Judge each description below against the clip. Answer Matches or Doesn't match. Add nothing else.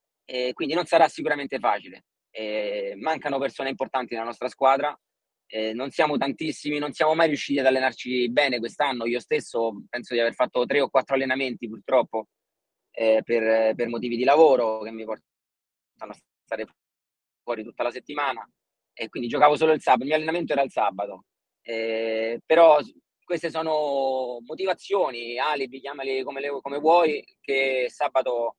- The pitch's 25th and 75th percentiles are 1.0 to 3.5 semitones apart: Doesn't match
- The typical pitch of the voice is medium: Doesn't match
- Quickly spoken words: Doesn't match